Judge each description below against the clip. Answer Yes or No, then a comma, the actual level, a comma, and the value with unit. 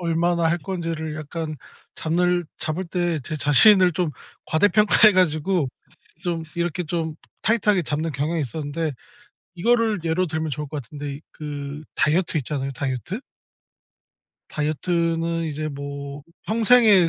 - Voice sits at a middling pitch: Yes, medium, 165 Hz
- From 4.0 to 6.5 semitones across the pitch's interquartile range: No, average, 3.1 semitones